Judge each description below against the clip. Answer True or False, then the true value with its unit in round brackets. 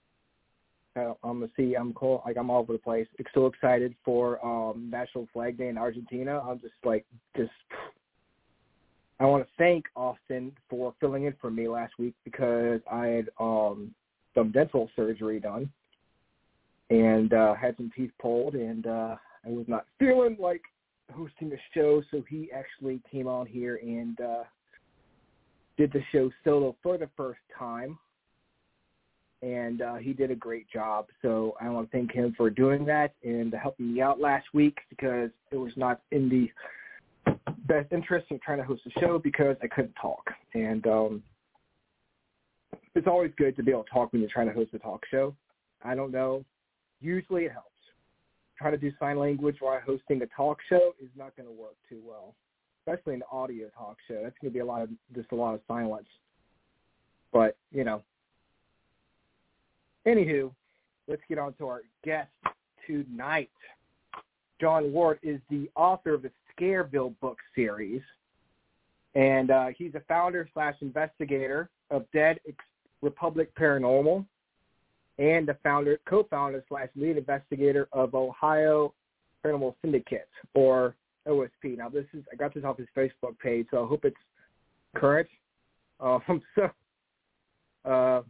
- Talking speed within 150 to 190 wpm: True (160 wpm)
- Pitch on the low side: True (130 Hz)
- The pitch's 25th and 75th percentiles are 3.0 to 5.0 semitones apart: True (3.6 semitones)